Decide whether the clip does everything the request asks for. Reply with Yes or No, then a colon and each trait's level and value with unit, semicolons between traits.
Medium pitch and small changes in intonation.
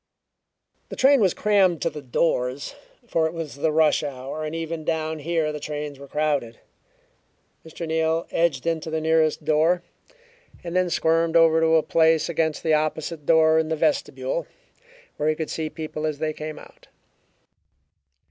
Yes: medium, 160 Hz; narrow, 1.3 semitones